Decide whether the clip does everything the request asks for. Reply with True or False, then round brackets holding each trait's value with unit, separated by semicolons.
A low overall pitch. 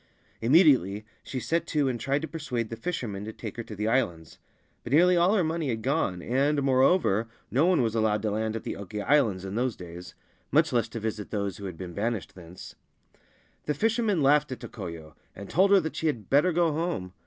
True (120 Hz)